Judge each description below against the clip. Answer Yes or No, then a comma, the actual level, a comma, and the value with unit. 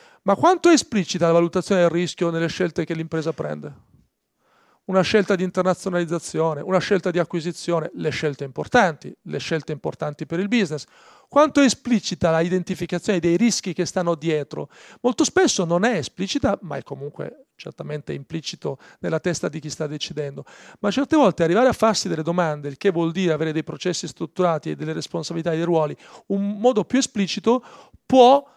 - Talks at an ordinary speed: No, fast, 175 wpm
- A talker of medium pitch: Yes, medium, 175 Hz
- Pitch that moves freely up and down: No, average, 4.1 semitones